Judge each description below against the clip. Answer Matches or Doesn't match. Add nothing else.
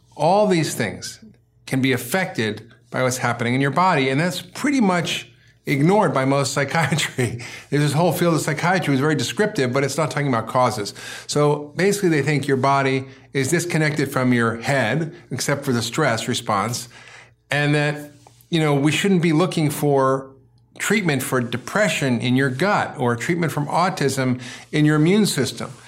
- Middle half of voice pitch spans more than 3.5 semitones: Matches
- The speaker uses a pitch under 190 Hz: Matches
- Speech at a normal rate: Matches